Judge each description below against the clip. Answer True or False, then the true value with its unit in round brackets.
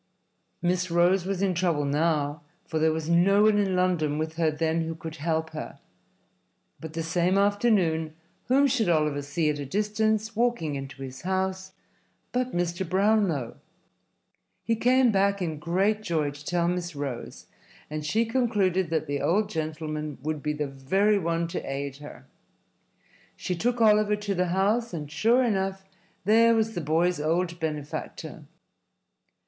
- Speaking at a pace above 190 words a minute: False (160 wpm)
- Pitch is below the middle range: False (175 Hz)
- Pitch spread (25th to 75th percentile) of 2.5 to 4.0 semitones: False (4.7 semitones)